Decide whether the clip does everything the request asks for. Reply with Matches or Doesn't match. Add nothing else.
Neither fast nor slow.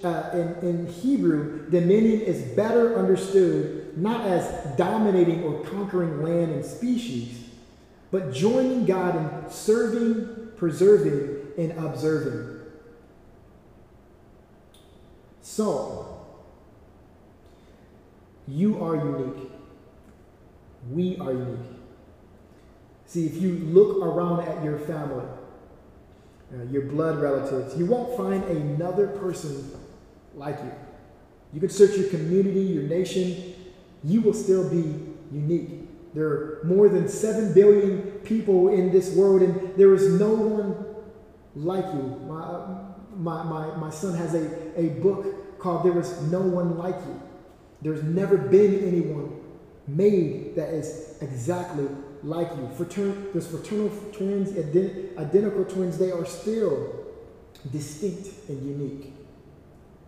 Doesn't match